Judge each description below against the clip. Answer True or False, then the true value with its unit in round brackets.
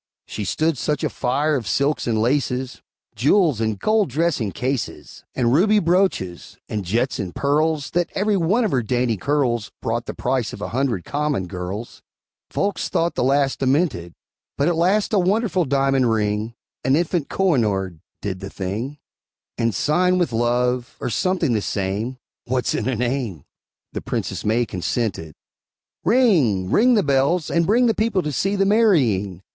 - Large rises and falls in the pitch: True (7.3 semitones)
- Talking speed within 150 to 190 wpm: True (165 wpm)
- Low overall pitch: True (130 Hz)